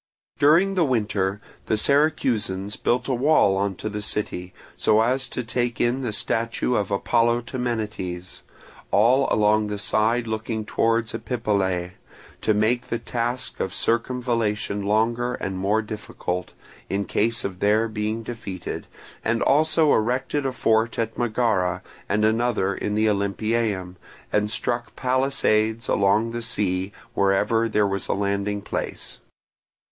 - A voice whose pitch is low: Yes, low, 110 Hz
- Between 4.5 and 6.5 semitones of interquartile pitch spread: No, average, 2.9 semitones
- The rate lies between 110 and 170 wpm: Yes, average, 140 wpm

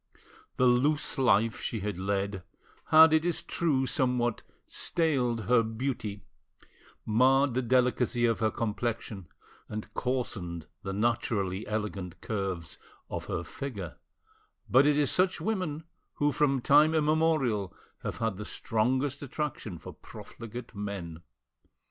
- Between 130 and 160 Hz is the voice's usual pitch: No, low, 120 Hz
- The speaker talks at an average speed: No, slow, 125 wpm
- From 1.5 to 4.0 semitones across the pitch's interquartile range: No, average, 5.2 semitones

